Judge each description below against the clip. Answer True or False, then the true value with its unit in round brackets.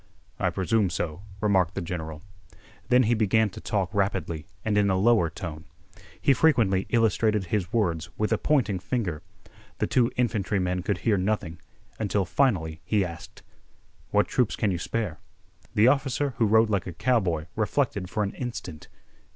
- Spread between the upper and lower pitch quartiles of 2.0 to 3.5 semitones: False (4.1 semitones)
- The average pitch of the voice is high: False (100 Hz)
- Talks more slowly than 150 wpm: False (160 wpm)